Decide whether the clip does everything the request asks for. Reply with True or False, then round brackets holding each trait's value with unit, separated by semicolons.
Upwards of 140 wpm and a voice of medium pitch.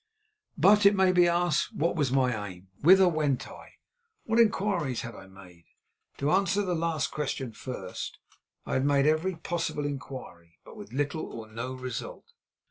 True (165 wpm; 145 Hz)